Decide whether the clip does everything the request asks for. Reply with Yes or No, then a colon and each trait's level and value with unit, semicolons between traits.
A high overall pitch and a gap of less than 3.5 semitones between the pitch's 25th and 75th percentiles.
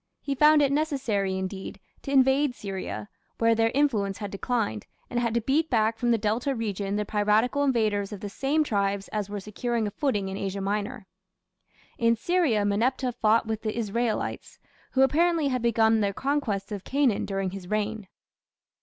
No: high, 220 Hz; average, 4.5 semitones